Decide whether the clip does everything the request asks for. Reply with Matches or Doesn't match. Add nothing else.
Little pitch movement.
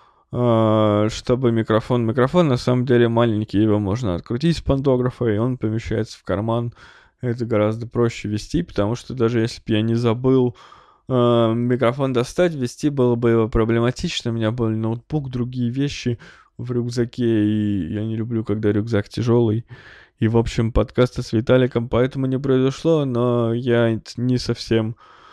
Matches